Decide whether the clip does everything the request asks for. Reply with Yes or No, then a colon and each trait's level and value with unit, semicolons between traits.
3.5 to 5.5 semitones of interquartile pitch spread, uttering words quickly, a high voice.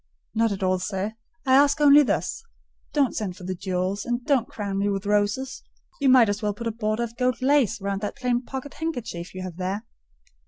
Yes: average, 4.7 semitones; fast, 210 wpm; high, 220 Hz